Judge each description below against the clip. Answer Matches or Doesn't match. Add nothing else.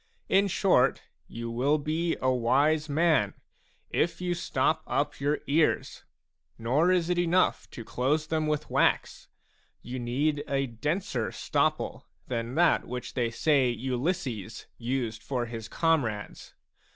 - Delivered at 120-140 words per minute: Matches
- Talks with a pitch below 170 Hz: Matches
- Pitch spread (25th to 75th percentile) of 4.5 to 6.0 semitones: Matches